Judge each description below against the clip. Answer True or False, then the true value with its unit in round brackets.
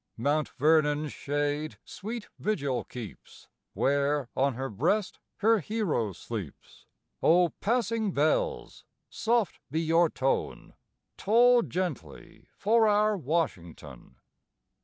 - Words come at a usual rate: False (100 wpm)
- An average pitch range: False (7.6 semitones)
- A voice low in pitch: False (155 Hz)